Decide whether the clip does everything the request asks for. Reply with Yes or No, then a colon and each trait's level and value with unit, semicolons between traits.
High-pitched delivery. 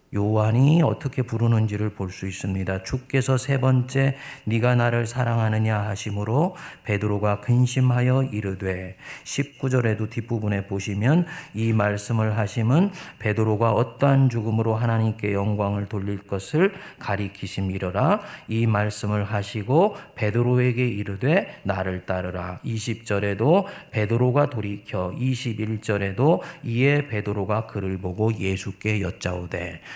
No: low, 110 Hz